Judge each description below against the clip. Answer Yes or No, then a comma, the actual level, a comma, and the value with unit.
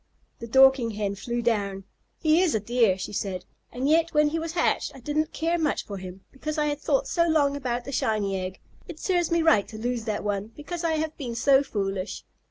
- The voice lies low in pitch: No, very high, 255 Hz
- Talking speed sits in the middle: No, fast, 225 wpm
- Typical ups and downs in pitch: No, wide, 6.9 semitones